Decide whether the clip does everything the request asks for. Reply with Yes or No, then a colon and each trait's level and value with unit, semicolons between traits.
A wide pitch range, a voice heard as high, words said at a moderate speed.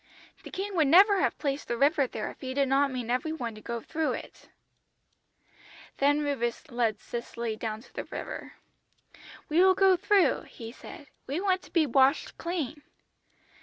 Yes: wide, 6.0 semitones; very high, 280 Hz; average, 175 wpm